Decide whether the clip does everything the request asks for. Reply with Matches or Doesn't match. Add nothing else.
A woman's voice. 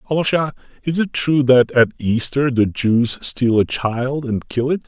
Doesn't match